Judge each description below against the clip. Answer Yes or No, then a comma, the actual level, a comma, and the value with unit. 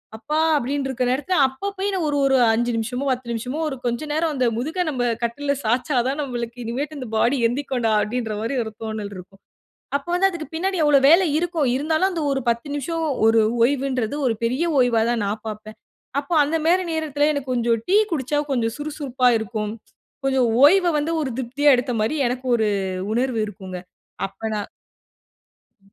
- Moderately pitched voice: No, very high, 260 Hz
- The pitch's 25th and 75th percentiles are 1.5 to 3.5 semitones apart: No, average, 4.3 semitones